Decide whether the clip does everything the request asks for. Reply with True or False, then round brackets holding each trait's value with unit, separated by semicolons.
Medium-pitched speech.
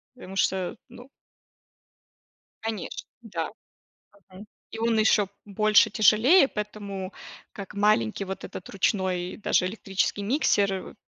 False (205 Hz)